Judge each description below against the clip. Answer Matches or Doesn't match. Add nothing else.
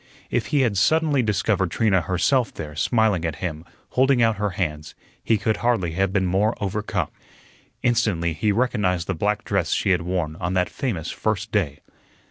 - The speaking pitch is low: Matches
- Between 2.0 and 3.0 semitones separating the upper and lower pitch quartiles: Doesn't match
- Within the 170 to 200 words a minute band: Matches